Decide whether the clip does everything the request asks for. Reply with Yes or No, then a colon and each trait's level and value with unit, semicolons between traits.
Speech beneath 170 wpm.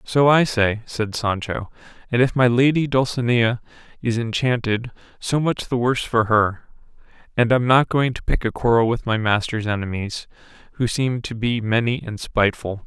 No: average, 175 wpm